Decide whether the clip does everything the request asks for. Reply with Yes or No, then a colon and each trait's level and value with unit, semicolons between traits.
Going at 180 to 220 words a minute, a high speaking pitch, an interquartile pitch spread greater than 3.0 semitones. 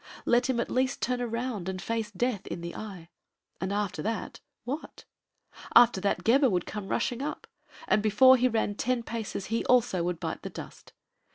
Yes: average, 185 wpm; high, 230 Hz; average, 3.7 semitones